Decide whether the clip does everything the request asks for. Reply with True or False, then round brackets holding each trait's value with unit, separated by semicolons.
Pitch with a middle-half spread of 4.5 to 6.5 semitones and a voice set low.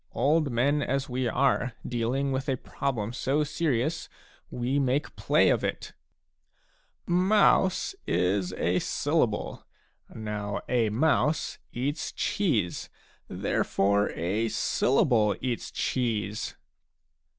True (4.8 semitones; 125 Hz)